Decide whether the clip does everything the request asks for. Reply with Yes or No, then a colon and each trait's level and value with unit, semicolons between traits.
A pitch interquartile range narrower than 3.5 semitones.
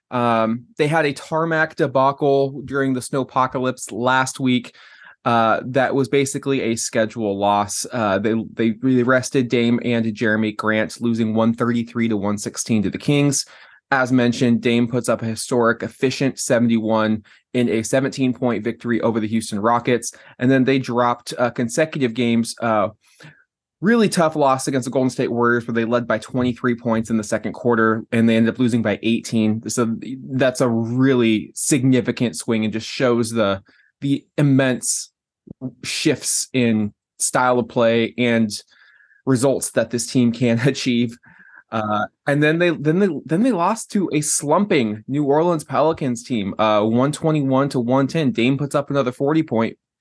Yes: average, 3.0 semitones